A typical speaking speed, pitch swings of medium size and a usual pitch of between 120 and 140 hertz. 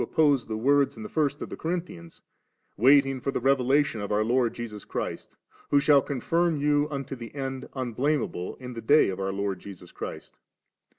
No: fast, 210 wpm; average, 4.3 semitones; low, 135 Hz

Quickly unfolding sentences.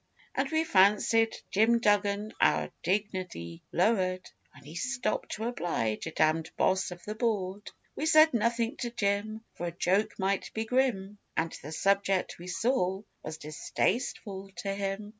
No: average, 155 wpm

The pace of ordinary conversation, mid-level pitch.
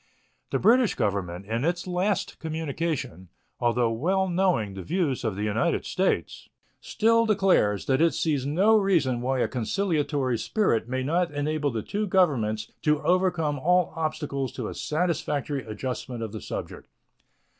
Yes: average, 150 wpm; medium, 150 Hz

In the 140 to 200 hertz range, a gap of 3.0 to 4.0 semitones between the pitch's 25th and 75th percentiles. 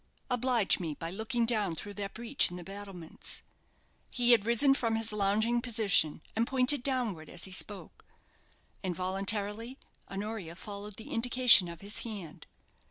No: high, 210 Hz; average, 3.6 semitones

